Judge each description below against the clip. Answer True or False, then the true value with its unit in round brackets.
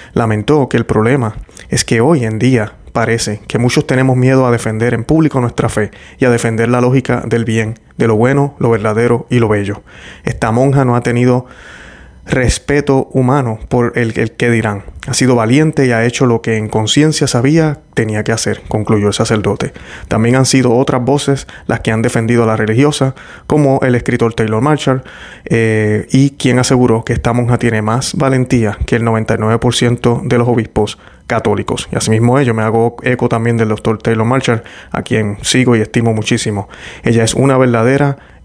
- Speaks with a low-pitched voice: True (120 Hz)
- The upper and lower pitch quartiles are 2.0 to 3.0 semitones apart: True (2.7 semitones)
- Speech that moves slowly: False (185 wpm)